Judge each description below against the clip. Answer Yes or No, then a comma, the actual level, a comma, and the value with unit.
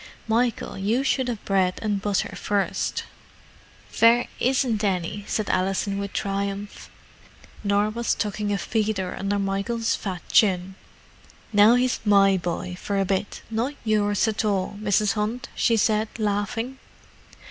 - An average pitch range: No, narrow, 2.2 semitones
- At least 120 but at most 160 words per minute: Yes, slow, 135 wpm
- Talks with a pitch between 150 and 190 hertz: No, high, 205 Hz